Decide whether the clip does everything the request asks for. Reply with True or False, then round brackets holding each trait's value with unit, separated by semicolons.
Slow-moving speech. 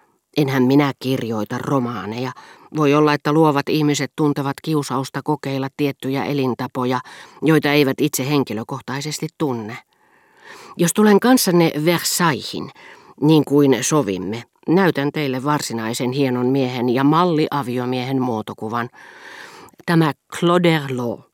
False (105 wpm)